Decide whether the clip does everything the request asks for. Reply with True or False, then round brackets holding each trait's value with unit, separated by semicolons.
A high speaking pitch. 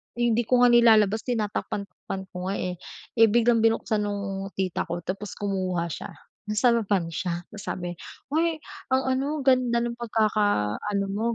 True (210 Hz)